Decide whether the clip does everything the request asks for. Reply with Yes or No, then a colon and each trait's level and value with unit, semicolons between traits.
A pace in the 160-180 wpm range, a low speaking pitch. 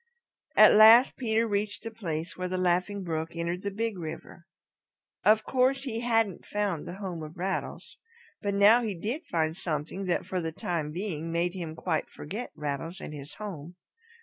No: average, 175 wpm; medium, 185 Hz